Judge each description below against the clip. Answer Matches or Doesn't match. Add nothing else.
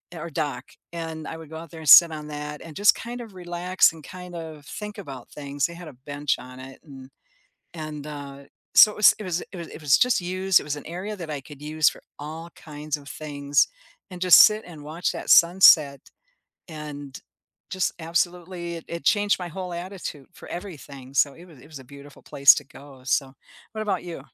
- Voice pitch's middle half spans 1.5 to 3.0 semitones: Doesn't match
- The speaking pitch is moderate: Matches